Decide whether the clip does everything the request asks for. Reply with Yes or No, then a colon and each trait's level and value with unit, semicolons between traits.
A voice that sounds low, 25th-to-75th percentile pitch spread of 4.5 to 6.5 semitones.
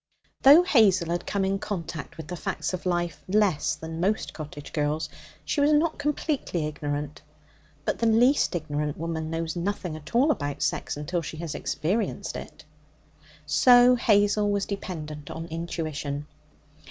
No: medium, 170 Hz; average, 5.3 semitones